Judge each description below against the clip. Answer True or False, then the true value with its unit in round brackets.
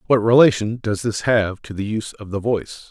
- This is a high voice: False (110 Hz)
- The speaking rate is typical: False (225 wpm)